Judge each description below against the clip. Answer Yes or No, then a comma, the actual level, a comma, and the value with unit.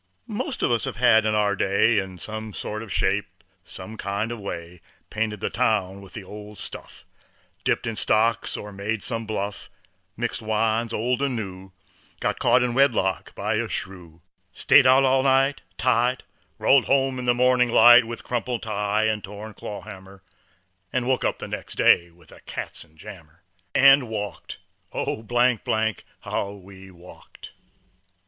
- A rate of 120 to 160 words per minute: Yes, average, 155 wpm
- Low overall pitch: Yes, low, 110 Hz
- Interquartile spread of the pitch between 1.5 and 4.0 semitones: Yes, average, 3.6 semitones